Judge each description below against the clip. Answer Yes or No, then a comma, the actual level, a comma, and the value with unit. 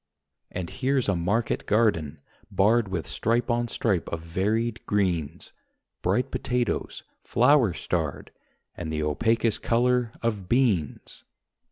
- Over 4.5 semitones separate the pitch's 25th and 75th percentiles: Yes, average, 5.3 semitones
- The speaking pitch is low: Yes, low, 110 Hz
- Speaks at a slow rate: Yes, slow, 120 wpm